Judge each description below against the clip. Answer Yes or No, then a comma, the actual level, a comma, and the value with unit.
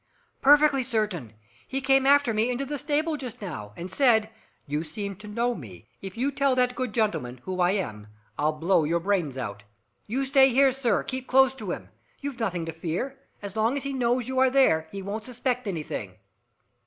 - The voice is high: Yes, high, 230 Hz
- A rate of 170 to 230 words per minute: Yes, average, 200 wpm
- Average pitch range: No, wide, 7.0 semitones